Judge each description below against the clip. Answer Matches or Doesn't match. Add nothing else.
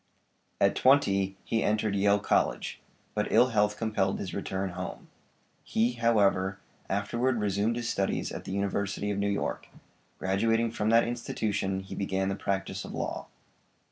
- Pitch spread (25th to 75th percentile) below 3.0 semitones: Matches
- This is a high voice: Doesn't match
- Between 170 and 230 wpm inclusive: Doesn't match